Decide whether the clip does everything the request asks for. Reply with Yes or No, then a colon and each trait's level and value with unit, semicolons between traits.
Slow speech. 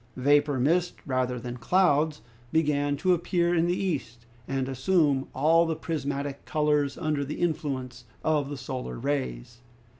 No: average, 145 wpm